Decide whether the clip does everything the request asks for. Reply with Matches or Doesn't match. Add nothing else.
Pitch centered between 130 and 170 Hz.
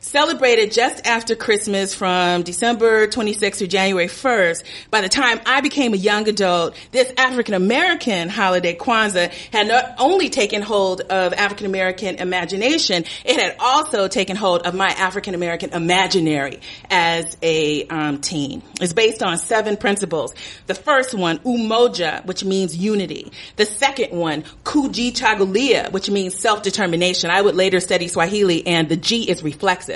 Doesn't match